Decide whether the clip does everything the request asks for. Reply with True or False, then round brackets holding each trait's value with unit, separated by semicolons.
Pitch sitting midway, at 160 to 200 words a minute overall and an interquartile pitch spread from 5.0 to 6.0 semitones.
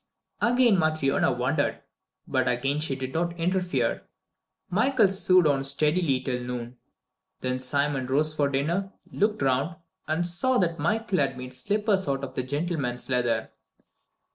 False (150 Hz; 140 wpm; 5.6 semitones)